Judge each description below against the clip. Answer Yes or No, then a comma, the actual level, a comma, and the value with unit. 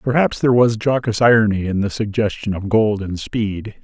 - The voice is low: Yes, low, 110 Hz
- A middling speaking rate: Yes, average, 190 wpm